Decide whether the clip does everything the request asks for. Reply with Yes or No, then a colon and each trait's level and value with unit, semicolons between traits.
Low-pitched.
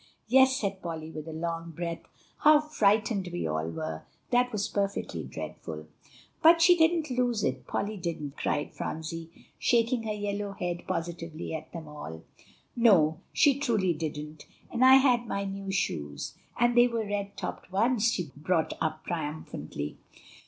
No: high, 190 Hz